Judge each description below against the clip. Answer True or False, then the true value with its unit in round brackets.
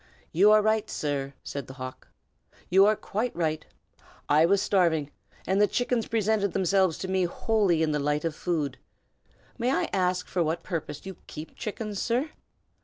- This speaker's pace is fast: False (175 wpm)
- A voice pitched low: False (185 Hz)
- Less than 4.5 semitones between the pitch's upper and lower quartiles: False (5.1 semitones)